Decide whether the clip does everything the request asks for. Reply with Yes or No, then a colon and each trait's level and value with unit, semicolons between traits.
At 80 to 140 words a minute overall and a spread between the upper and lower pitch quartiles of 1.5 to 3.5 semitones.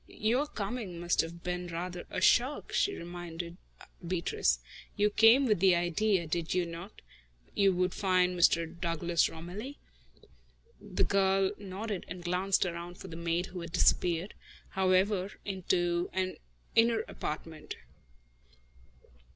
Yes: slow, 135 wpm; narrow, 2.5 semitones